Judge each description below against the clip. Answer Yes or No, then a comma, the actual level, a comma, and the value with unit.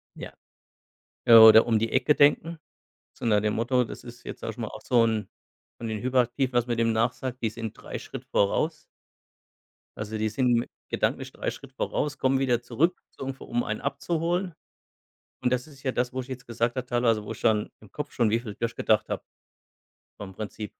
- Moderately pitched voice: No, low, 120 Hz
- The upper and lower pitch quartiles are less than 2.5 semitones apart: No, average, 2.8 semitones